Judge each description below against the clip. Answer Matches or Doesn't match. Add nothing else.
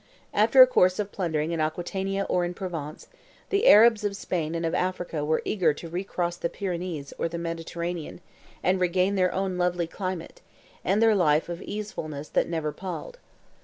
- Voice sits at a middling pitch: Matches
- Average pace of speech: Matches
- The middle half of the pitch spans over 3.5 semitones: Doesn't match